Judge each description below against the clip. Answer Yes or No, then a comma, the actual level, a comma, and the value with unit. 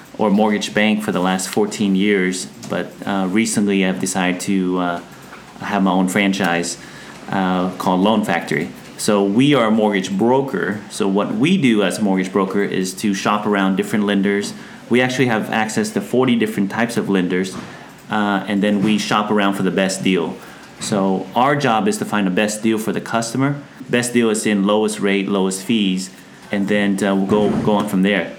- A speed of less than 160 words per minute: No, average, 195 wpm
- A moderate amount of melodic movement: No, narrow, 2.0 semitones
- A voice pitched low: Yes, low, 100 Hz